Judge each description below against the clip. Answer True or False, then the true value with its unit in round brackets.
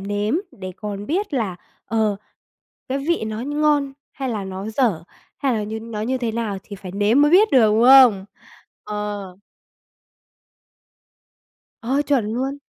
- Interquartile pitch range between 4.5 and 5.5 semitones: True (4.8 semitones)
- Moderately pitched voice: False (225 Hz)